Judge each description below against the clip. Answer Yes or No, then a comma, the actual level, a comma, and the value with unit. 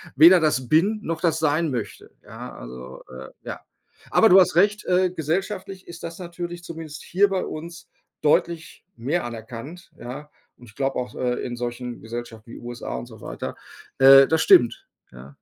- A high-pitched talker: No, medium, 150 Hz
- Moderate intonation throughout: No, wide, 6.3 semitones